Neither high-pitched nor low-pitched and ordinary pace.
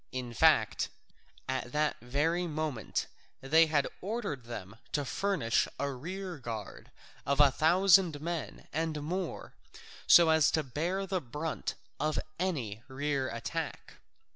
No: medium, 150 Hz; slow, 130 wpm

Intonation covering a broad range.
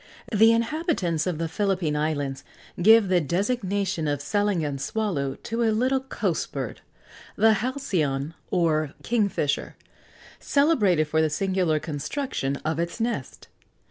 Yes: wide, 6.4 semitones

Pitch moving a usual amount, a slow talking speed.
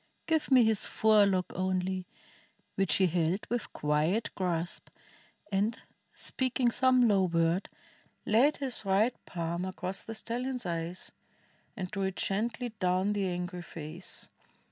Yes: average, 4.0 semitones; slow, 130 wpm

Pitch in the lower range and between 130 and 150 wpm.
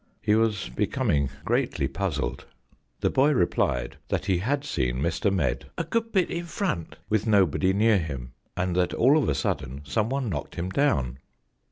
No: very low, 95 Hz; average, 170 wpm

